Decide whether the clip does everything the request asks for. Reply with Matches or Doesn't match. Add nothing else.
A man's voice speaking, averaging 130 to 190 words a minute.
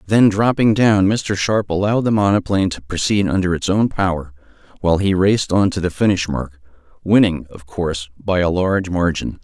Matches